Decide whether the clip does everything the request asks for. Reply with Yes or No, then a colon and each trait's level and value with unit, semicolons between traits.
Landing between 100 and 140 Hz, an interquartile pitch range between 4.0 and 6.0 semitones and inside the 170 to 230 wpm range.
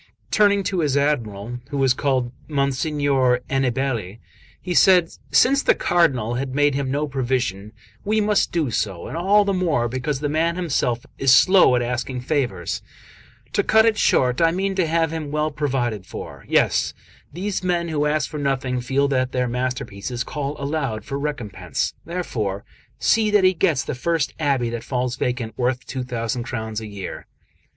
Yes: low, 135 Hz; average, 4.9 semitones; average, 175 wpm